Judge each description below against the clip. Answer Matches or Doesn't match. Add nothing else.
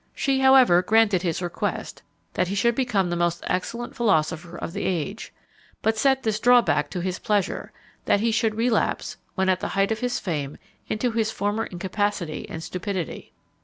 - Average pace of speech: Matches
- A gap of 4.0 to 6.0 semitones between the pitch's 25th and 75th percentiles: Matches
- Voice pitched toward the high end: Matches